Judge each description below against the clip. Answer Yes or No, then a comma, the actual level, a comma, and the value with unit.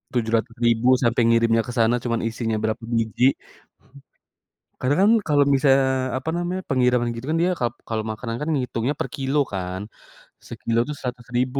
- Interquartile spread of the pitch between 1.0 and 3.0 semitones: Yes, average, 2.7 semitones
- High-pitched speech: No, low, 120 Hz